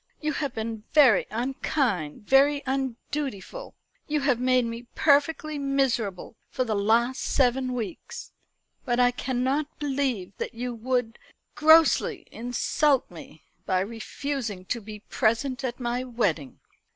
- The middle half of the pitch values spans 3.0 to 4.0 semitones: Yes, average, 3.6 semitones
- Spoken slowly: Yes, slow, 125 wpm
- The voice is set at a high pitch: Yes, very high, 250 Hz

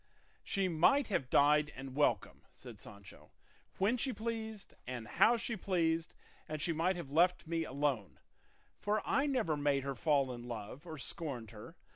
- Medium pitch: Yes, medium, 155 Hz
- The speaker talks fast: No, average, 165 wpm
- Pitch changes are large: Yes, wide, 6.0 semitones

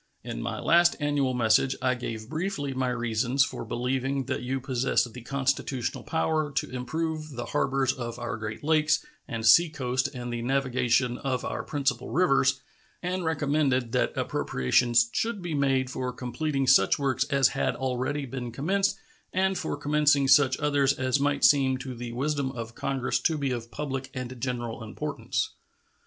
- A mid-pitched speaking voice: No, low, 130 Hz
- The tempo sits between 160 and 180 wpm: Yes, average, 165 wpm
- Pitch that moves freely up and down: No, average, 2.9 semitones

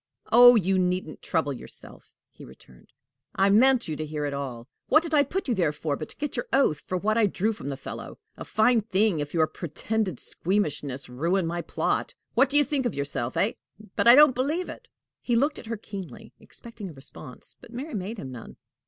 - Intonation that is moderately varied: No, wide, 8.1 semitones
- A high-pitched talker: Yes, high, 195 Hz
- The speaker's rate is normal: No, fast, 215 wpm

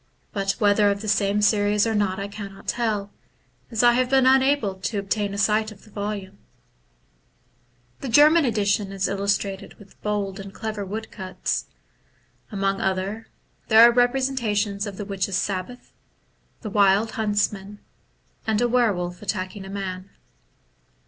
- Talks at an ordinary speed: Yes, average, 150 wpm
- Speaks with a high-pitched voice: Yes, high, 205 Hz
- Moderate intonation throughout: No, narrow, 2.1 semitones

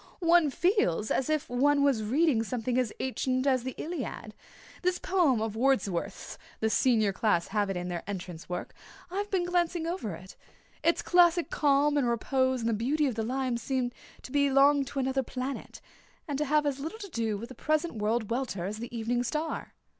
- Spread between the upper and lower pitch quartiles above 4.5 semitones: Yes, average, 5.2 semitones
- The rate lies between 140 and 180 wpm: No, average, 190 wpm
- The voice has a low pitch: No, very high, 260 Hz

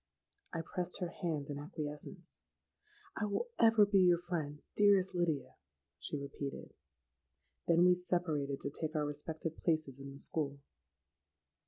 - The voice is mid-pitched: Yes, medium, 160 Hz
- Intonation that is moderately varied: Yes, average, 4.1 semitones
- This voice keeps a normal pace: No, slow, 130 wpm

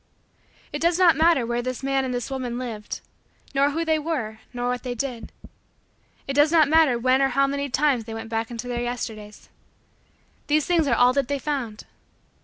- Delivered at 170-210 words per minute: Yes, average, 200 wpm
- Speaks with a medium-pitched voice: No, very high, 260 Hz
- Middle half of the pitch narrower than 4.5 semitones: Yes, average, 3.4 semitones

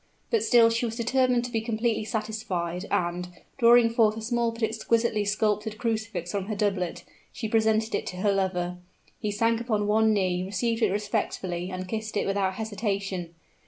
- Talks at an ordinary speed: Yes, average, 175 wpm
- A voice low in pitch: No, high, 215 Hz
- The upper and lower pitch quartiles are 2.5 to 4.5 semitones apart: Yes, average, 2.9 semitones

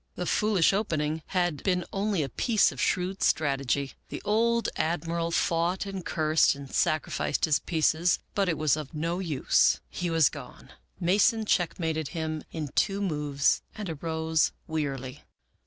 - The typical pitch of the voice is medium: Yes, medium, 165 Hz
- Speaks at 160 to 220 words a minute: No, average, 150 wpm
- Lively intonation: No, average, 3.3 semitones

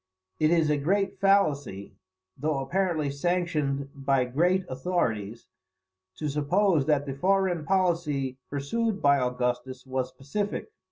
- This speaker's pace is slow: Yes, slow, 120 wpm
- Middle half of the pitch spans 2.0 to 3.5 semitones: No, average, 5.1 semitones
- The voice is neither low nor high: Yes, medium, 145 Hz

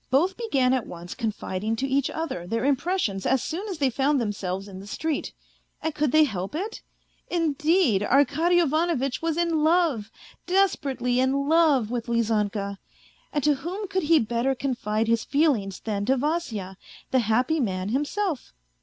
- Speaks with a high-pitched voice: Yes, very high, 270 Hz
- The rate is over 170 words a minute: No, average, 165 wpm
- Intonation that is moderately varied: No, wide, 6.4 semitones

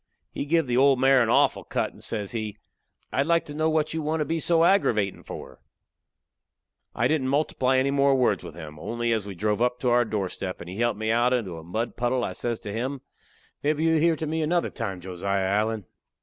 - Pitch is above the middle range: No, low, 120 Hz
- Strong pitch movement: Yes, wide, 5.9 semitones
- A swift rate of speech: Yes, fast, 225 wpm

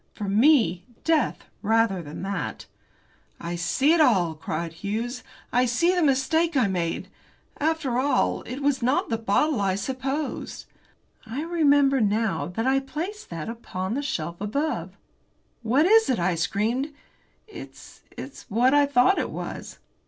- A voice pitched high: Yes, high, 245 Hz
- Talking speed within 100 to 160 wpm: Yes, average, 150 wpm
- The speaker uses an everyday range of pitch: No, wide, 6.5 semitones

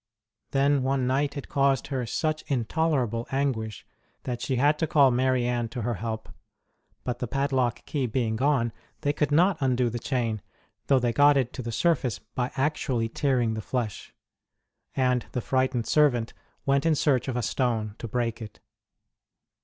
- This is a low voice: Yes, low, 130 Hz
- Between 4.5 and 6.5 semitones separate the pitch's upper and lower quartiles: No, average, 2.9 semitones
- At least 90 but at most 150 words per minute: No, average, 170 wpm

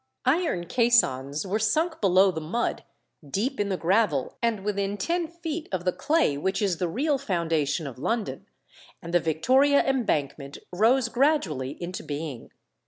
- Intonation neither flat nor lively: No, wide, 8.1 semitones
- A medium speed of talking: Yes, average, 155 wpm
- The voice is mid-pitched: No, high, 195 Hz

